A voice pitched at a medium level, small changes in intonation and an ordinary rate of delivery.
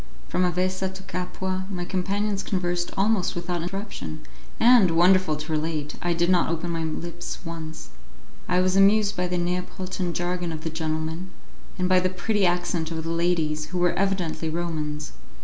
Yes: medium, 175 Hz; narrow, 2.2 semitones; average, 165 wpm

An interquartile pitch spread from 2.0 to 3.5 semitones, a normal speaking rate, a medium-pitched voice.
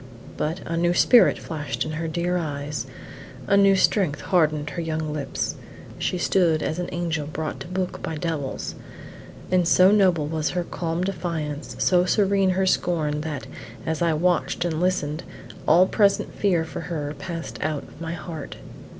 Yes: average, 2.7 semitones; average, 165 wpm; medium, 165 Hz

